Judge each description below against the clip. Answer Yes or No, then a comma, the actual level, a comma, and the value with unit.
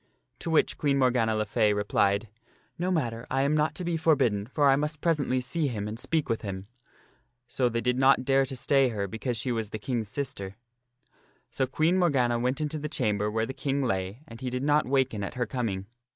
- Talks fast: Yes, fast, 225 wpm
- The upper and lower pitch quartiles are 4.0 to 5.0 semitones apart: Yes, average, 4.3 semitones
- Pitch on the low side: Yes, low, 125 Hz